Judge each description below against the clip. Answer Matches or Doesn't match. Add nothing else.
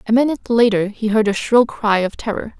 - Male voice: Doesn't match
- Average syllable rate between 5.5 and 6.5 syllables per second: Matches